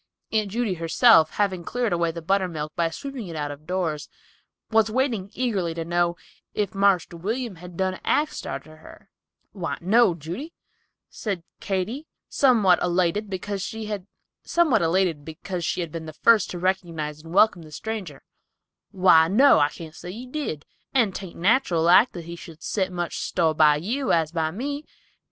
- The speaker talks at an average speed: Yes, average, 160 wpm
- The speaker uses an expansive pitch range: No, average, 4.7 semitones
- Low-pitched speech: No, medium, 185 Hz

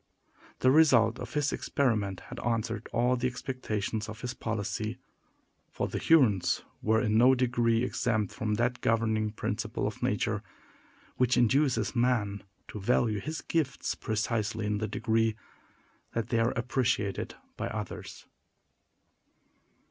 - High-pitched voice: No, low, 115 Hz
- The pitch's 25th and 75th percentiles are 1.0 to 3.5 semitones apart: Yes, narrow, 2.6 semitones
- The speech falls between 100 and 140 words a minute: Yes, slow, 135 wpm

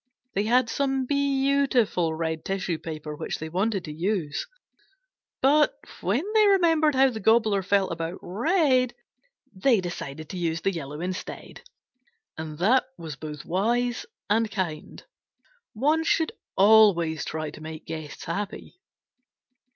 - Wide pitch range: Yes, wide, 7.9 semitones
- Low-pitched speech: No, high, 195 Hz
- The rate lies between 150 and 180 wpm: No, slow, 135 wpm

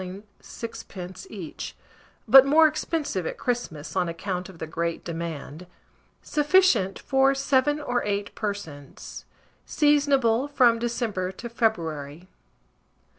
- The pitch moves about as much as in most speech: No, wide, 7.2 semitones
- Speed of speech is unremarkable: No, slow, 110 wpm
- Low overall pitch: No, high, 215 Hz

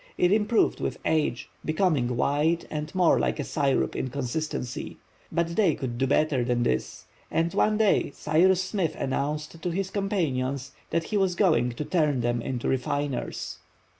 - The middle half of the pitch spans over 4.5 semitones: Yes, average, 5.3 semitones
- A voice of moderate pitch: Yes, medium, 155 Hz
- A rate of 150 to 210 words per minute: Yes, average, 165 wpm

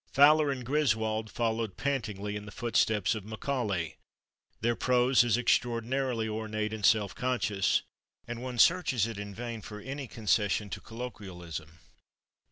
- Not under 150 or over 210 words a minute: No, average, 140 wpm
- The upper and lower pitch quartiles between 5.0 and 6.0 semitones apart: No, average, 3.1 semitones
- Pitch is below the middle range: Yes, low, 110 Hz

